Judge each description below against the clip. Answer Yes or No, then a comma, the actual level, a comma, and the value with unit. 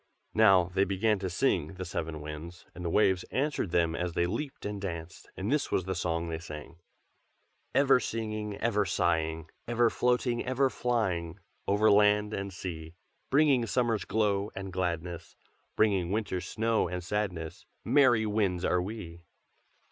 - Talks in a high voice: No, very low, 95 Hz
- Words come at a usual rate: Yes, average, 155 wpm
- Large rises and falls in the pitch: No, average, 4.4 semitones